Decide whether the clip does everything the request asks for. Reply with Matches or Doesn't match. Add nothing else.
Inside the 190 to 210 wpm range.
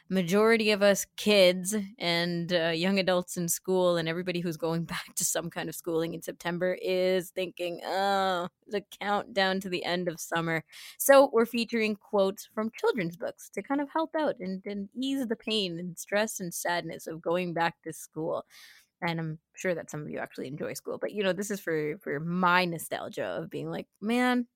Matches